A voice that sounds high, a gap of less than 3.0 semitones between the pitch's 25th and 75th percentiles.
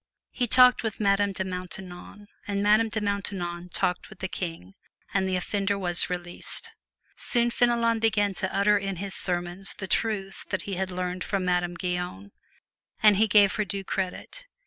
Yes: high, 195 Hz; narrow, 2.5 semitones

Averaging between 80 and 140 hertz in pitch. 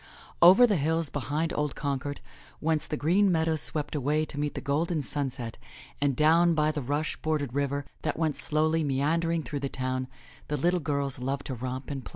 No: medium, 150 Hz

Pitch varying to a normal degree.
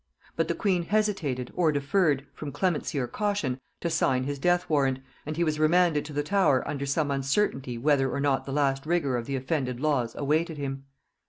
Yes: average, 3.6 semitones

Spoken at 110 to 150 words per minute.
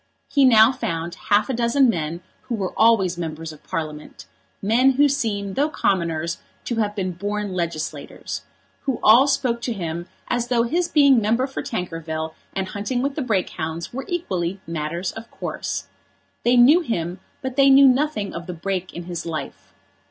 No: average, 175 wpm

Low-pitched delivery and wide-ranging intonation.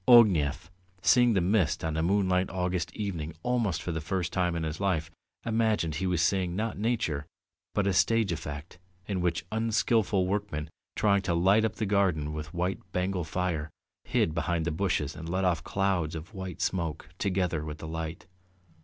No: very low, 90 Hz; average, 3.7 semitones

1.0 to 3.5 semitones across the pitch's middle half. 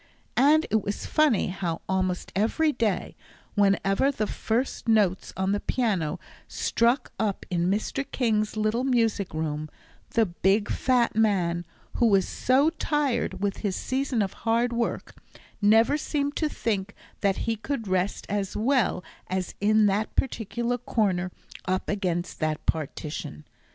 No: average, 4.1 semitones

